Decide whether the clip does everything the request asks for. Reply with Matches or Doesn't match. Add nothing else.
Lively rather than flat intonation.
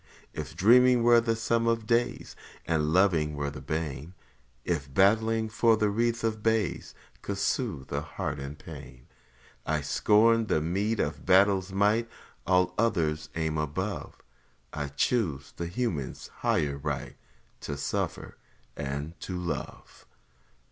Matches